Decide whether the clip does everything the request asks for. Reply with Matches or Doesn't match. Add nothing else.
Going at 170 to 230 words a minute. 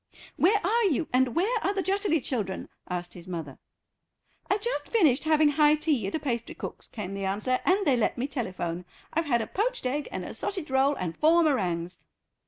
Matches